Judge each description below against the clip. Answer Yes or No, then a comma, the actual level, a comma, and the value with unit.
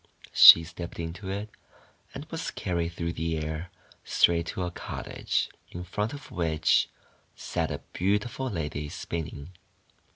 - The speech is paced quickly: No, slow, 135 wpm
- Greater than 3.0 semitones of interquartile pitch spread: No, narrow, 2.5 semitones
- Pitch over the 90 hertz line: No, very low, 85 Hz